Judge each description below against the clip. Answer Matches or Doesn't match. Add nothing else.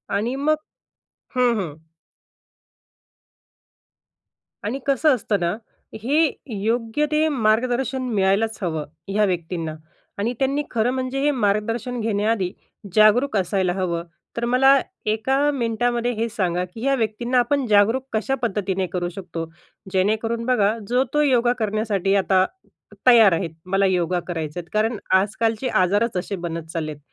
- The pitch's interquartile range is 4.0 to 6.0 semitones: Matches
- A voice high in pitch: Matches